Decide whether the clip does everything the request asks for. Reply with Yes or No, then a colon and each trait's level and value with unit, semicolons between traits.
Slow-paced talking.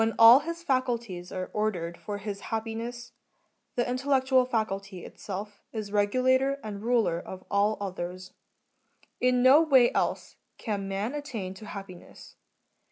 Yes: slow, 130 wpm